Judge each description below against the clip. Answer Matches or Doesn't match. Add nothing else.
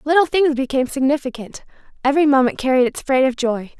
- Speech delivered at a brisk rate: Doesn't match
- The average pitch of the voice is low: Doesn't match